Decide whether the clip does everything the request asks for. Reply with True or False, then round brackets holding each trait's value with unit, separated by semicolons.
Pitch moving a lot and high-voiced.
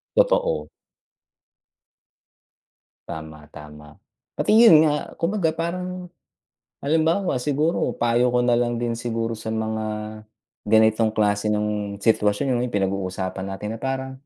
False (6.1 semitones; 115 Hz)